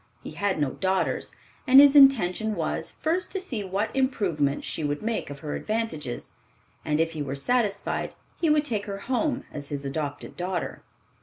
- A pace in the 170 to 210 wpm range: Yes, average, 175 wpm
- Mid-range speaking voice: No, high, 200 Hz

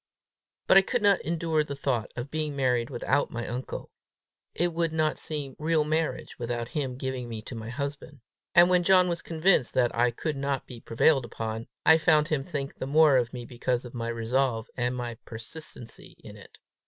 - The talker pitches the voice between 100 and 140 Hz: Yes, low, 135 Hz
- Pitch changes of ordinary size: Yes, average, 4.6 semitones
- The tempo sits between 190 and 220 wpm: Yes, average, 195 wpm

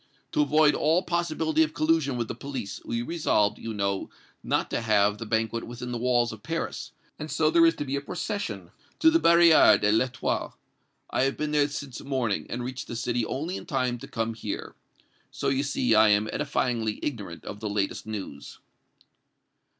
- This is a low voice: Yes, low, 125 Hz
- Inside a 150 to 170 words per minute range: No, average, 190 wpm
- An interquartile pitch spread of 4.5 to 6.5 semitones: Yes, average, 5.3 semitones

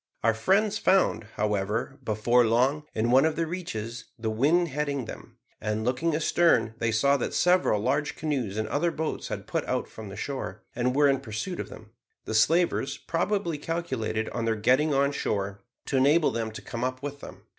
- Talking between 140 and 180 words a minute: No, average, 190 wpm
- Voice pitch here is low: Yes, low, 130 Hz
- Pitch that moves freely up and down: Yes, wide, 5.8 semitones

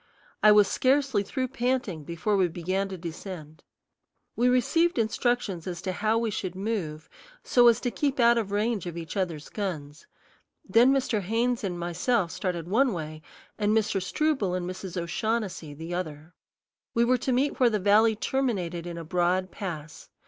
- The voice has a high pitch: Yes, high, 200 Hz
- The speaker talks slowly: No, average, 170 wpm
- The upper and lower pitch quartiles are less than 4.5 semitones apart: No, average, 5.2 semitones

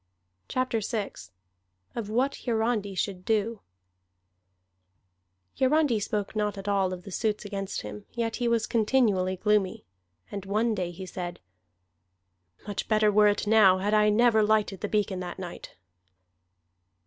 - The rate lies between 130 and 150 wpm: Yes, average, 140 wpm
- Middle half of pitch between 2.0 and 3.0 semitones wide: Yes, narrow, 2.4 semitones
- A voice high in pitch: Yes, high, 210 Hz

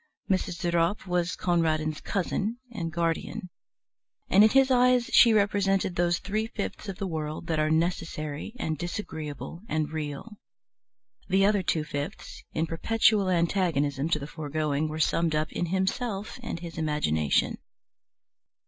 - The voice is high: No, medium, 170 Hz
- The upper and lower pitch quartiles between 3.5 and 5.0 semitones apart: Yes, average, 4.1 semitones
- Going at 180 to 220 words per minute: No, average, 145 wpm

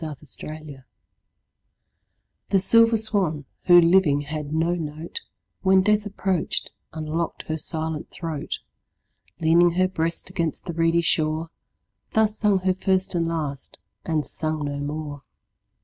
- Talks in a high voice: No, medium, 165 Hz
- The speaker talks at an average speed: No, slow, 130 wpm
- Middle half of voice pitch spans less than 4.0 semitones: Yes, average, 3.3 semitones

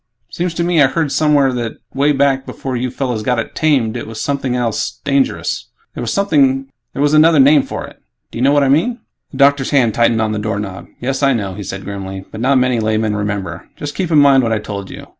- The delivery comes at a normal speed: No, fast, 230 wpm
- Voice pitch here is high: No, low, 130 Hz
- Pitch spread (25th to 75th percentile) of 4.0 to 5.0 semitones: Yes, average, 4.4 semitones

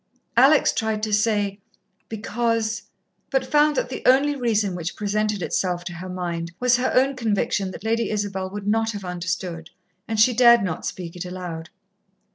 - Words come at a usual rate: Yes, average, 175 wpm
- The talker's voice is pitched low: No, high, 210 Hz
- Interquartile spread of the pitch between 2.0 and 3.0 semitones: No, average, 4.1 semitones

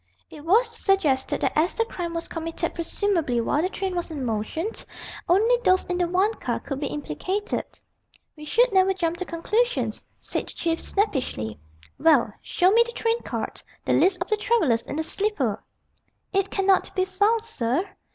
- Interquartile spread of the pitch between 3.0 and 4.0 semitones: No, average, 5.1 semitones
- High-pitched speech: Yes, very high, 360 Hz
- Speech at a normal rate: Yes, average, 180 wpm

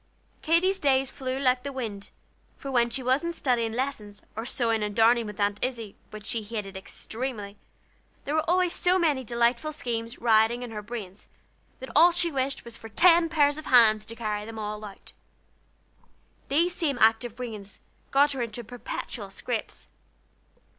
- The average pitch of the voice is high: Yes, high, 240 Hz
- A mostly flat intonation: No, average, 4.2 semitones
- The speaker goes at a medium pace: Yes, average, 165 wpm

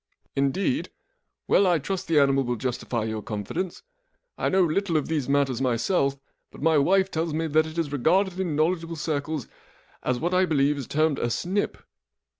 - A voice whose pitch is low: No, medium, 155 Hz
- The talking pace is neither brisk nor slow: Yes, average, 185 wpm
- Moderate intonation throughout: Yes, average, 4.2 semitones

